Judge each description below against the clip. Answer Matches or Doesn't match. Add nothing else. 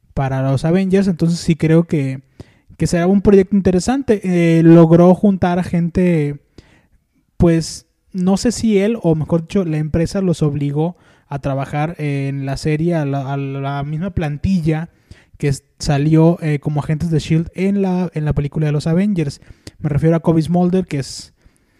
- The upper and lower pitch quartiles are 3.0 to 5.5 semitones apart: Matches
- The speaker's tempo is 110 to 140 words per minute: Doesn't match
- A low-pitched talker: Doesn't match